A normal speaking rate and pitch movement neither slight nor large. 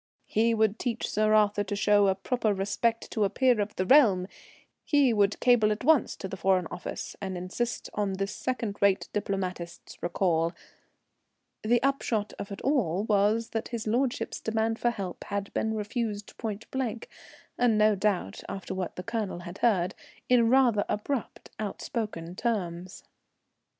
Yes: average, 155 wpm; average, 3.1 semitones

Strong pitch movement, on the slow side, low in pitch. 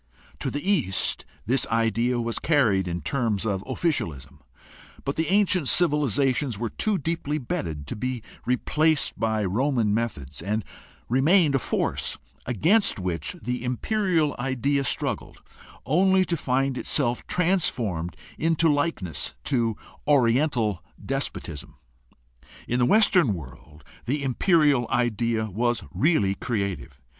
Yes: wide, 6.1 semitones; slow, 120 wpm; low, 125 Hz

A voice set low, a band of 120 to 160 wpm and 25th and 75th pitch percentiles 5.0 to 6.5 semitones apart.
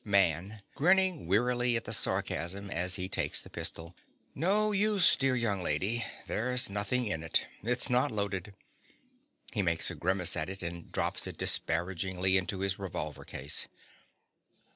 Yes: low, 100 Hz; average, 150 wpm; wide, 5.5 semitones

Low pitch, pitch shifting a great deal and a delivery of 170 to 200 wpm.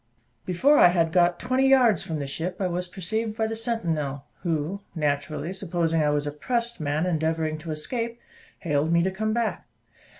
No: medium, 175 Hz; wide, 5.9 semitones; average, 185 wpm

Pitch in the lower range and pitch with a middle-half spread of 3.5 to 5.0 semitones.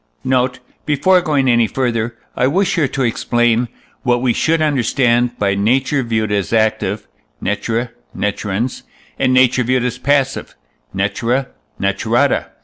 No: low, 120 Hz; average, 2.8 semitones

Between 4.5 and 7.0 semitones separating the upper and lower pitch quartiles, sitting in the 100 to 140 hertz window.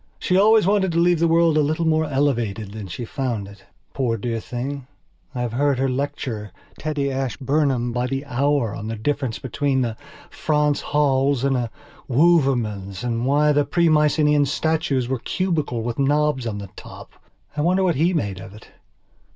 No: average, 4.1 semitones; low, 135 Hz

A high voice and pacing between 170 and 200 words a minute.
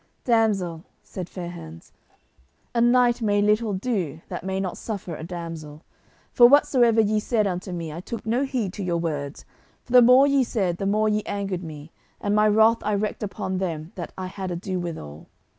Yes: high, 195 Hz; average, 190 wpm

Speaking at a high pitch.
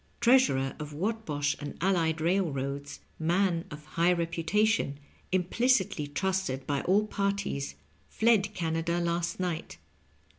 No: medium, 170 Hz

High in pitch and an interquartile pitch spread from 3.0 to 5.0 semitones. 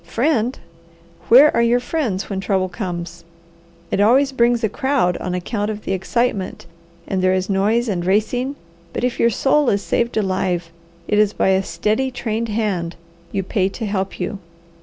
Yes: high, 210 Hz; average, 4.1 semitones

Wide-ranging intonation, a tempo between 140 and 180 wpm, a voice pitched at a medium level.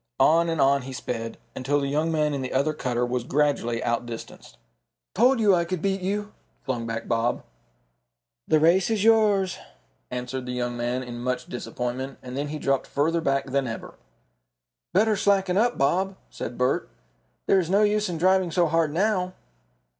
Yes: wide, 6.9 semitones; average, 175 wpm; medium, 150 Hz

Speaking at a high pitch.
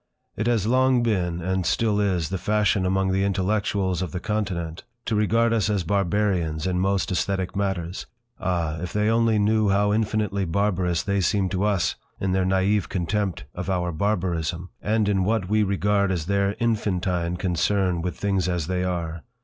No: very low, 95 Hz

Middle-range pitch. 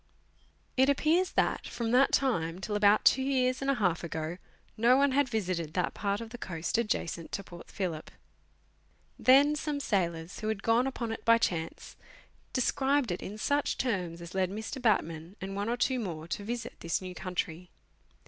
No: high, 210 Hz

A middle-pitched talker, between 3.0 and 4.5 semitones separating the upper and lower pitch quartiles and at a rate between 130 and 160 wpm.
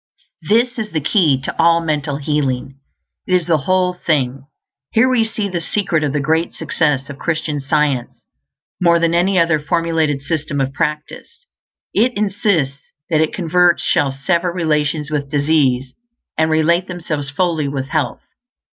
Yes: medium, 160 Hz; average, 3.7 semitones; average, 155 wpm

